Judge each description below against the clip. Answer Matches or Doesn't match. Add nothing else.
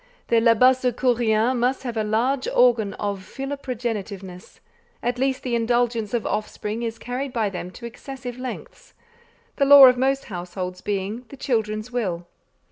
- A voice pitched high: Matches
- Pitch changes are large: Doesn't match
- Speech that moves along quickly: Doesn't match